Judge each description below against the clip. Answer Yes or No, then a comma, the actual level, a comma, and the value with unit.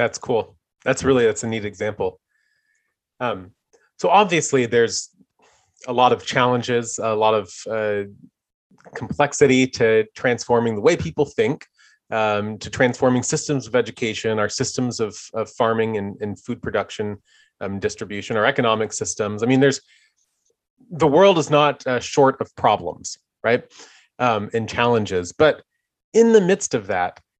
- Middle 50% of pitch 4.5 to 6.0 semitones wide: Yes, average, 5.3 semitones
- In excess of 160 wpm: No, average, 150 wpm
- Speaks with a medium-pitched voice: No, low, 120 Hz